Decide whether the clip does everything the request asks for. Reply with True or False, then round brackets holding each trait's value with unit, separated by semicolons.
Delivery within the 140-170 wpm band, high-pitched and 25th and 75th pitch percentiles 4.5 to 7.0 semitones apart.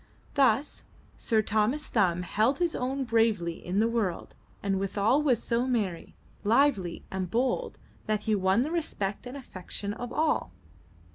True (150 wpm; 220 Hz; 5.0 semitones)